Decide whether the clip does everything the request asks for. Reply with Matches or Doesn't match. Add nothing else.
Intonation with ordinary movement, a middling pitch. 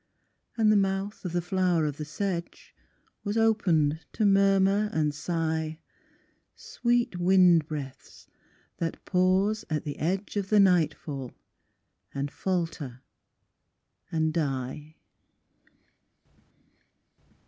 Matches